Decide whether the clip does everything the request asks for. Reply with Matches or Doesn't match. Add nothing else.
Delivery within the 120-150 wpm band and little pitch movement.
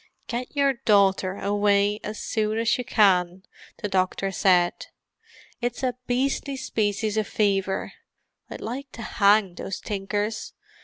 Doesn't match